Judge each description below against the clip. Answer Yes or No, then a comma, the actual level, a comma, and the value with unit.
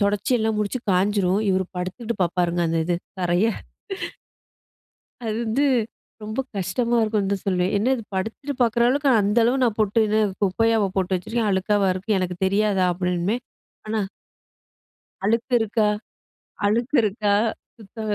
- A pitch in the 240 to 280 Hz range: No, high, 210 Hz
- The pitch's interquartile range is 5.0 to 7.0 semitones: No, average, 3.2 semitones